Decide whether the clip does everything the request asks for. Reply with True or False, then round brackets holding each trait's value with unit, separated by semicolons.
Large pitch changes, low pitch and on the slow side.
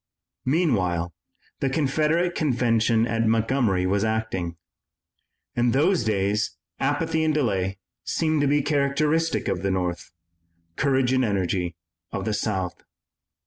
True (7.0 semitones; 115 Hz; 120 wpm)